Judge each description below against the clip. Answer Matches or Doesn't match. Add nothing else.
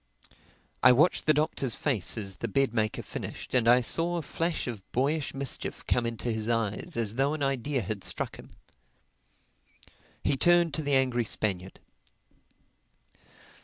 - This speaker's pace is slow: Doesn't match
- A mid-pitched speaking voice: Doesn't match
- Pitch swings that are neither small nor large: Matches